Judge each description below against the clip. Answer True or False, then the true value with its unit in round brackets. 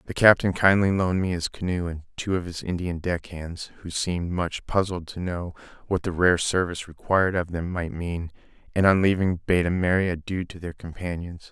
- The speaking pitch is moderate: False (90 Hz)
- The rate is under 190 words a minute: False (205 wpm)